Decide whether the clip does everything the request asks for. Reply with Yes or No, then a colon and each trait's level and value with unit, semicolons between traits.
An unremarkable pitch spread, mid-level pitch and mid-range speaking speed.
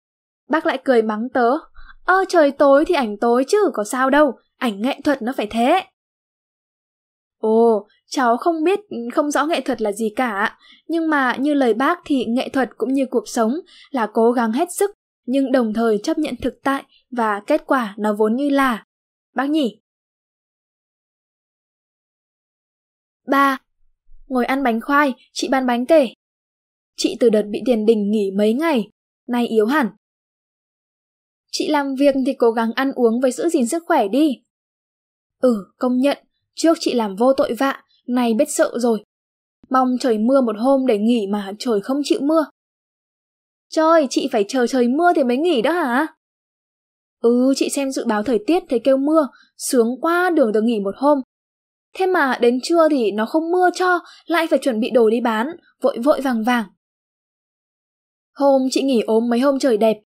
No: average, 4.5 semitones; very high, 265 Hz; average, 180 wpm